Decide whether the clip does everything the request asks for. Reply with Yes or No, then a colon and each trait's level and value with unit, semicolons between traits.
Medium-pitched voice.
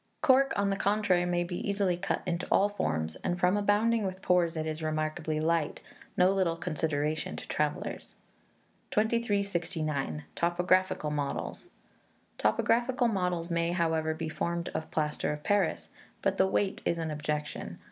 Yes: medium, 170 Hz